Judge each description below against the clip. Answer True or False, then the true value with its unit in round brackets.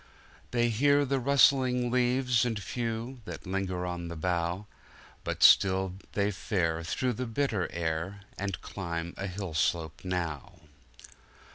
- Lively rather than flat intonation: True (5.9 semitones)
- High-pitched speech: False (100 Hz)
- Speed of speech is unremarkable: False (130 wpm)